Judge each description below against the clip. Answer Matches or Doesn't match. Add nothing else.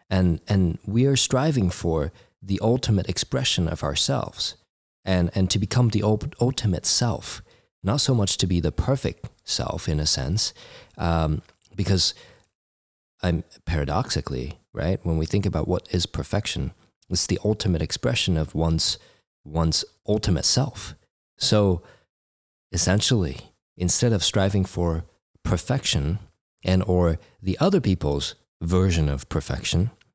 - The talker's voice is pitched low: Matches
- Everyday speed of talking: Doesn't match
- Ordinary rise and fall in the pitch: Matches